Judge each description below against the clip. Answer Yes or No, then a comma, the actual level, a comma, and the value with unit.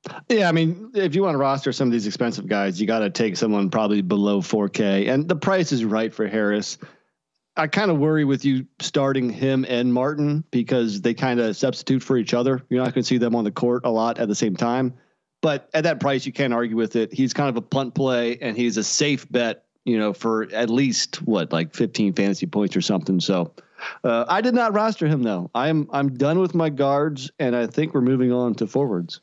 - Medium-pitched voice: No, low, 125 Hz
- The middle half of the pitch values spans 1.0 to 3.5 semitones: No, average, 4.0 semitones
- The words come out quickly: Yes, fast, 235 wpm